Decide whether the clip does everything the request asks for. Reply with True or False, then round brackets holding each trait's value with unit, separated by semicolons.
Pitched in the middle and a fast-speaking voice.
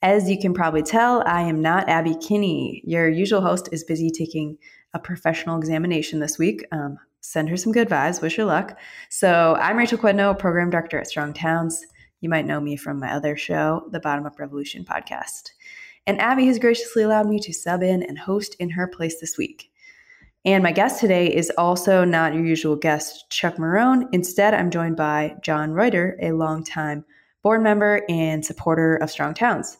False (170 Hz; 190 wpm)